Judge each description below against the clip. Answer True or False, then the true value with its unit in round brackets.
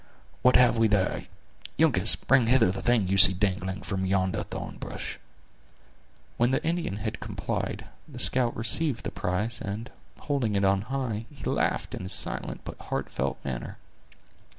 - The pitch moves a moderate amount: True (4.4 semitones)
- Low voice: True (110 Hz)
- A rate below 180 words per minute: True (160 wpm)